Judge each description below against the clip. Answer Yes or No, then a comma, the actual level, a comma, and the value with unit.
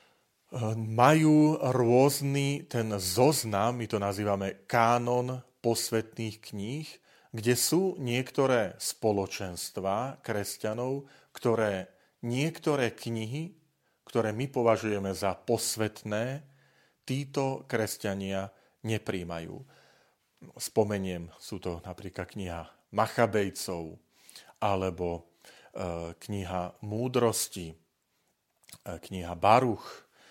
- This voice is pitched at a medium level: No, low, 110 Hz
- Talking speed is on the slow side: Yes, slow, 75 wpm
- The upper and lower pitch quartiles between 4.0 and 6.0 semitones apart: Yes, average, 4.4 semitones